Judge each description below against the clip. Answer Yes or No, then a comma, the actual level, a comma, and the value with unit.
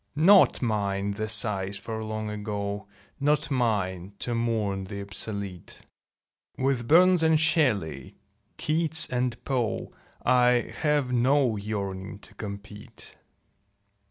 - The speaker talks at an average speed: No, slow, 110 wpm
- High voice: No, low, 110 Hz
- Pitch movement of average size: Yes, average, 4.2 semitones